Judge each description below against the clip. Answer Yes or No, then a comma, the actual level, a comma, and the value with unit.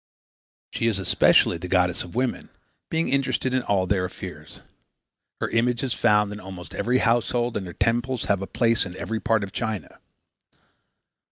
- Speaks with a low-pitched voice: Yes, low, 105 Hz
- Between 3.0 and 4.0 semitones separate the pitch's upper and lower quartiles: No, average, 4.4 semitones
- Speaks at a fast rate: No, average, 170 wpm